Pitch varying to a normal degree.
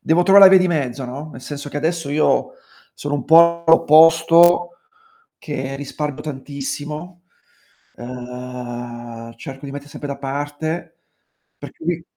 Yes: average, 3.7 semitones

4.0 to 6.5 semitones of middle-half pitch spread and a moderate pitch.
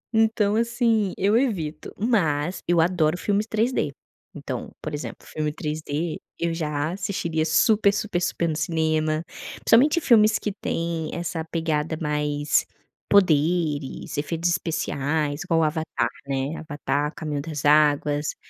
Yes: average, 4.4 semitones; medium, 160 Hz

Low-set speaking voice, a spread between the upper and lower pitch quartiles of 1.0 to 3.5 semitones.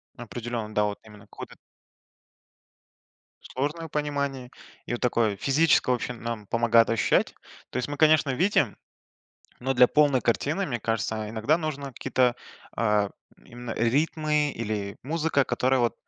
No: low, 125 Hz; average, 4.3 semitones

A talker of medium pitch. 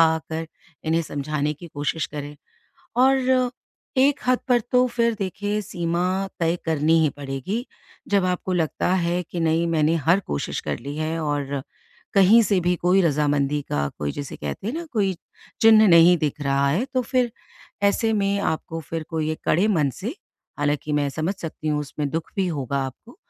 Yes: medium, 165 Hz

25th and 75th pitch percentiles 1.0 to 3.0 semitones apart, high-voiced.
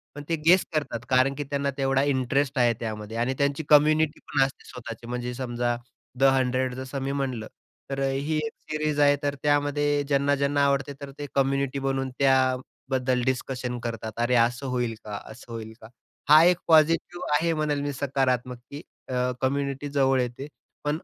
No: narrow, 2.4 semitones; low, 135 Hz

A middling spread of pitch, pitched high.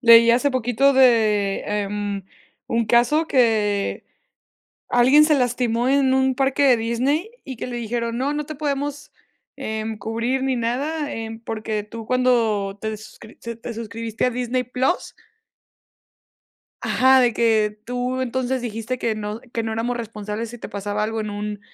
Yes: average, 3.0 semitones; high, 235 Hz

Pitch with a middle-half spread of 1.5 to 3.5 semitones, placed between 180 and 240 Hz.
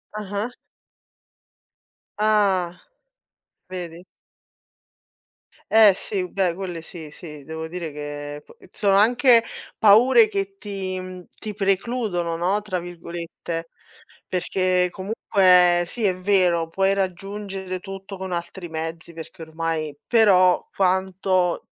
Yes: average, 2.7 semitones; medium, 185 Hz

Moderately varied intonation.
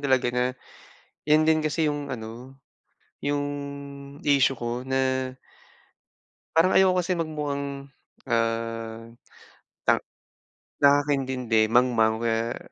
Yes: average, 3.8 semitones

